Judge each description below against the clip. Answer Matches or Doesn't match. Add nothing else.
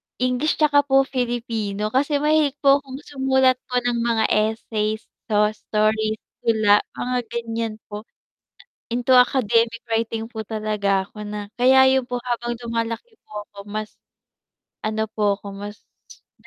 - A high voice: Matches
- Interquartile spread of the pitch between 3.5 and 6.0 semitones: Doesn't match